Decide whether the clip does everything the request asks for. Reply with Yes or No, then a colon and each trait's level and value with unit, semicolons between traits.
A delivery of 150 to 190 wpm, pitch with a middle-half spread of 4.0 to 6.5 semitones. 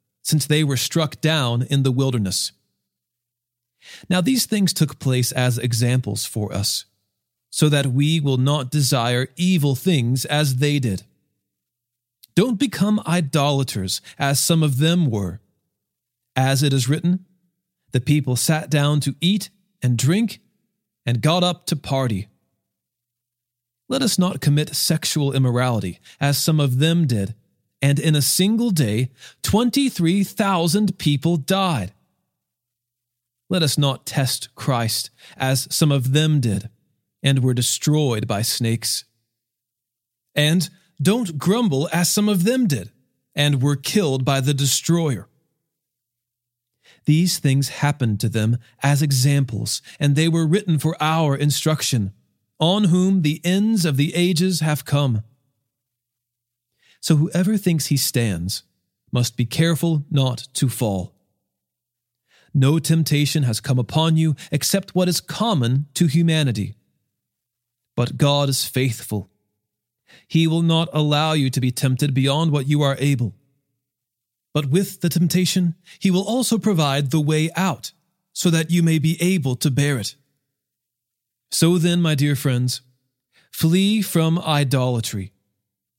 No: slow, 135 wpm; average, 5.3 semitones